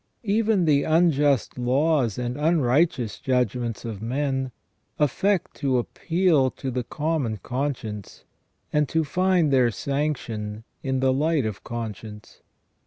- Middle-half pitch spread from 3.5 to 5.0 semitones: Yes, average, 4.6 semitones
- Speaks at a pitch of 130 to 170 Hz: Yes, low, 135 Hz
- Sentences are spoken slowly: Yes, slow, 120 wpm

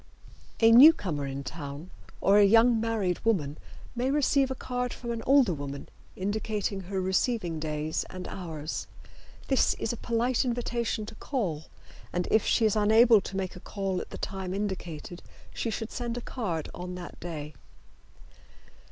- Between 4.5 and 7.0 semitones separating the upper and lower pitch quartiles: Yes, average, 5.1 semitones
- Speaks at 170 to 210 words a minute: No, average, 160 wpm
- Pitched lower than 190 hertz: No, high, 200 Hz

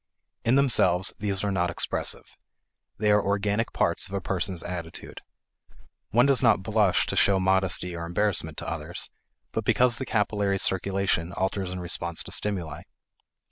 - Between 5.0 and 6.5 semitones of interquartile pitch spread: No, average, 2.7 semitones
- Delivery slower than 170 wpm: Yes, average, 155 wpm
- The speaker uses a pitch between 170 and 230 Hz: No, very low, 95 Hz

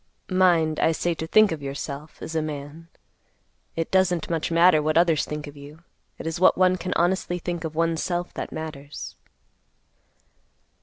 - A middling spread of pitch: No, narrow, 2.3 semitones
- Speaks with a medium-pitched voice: Yes, medium, 165 Hz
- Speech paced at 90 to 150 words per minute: No, average, 170 wpm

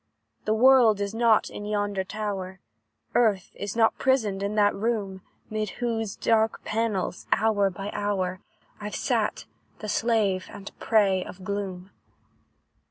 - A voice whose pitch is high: Yes, high, 205 Hz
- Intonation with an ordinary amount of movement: No, narrow, 2.2 semitones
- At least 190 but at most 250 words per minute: No, slow, 135 wpm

